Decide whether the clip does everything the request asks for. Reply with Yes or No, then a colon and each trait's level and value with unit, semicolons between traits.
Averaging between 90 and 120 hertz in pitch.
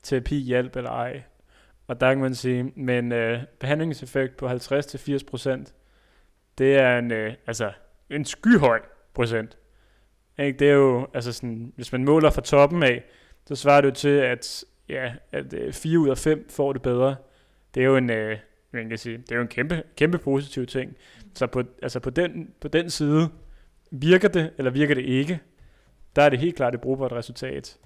No: low, 130 Hz